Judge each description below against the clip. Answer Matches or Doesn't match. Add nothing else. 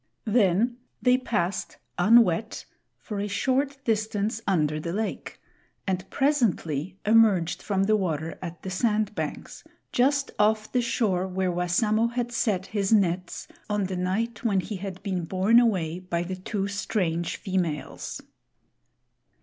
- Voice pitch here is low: Doesn't match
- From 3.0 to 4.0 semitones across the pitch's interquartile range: Matches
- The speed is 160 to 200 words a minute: Doesn't match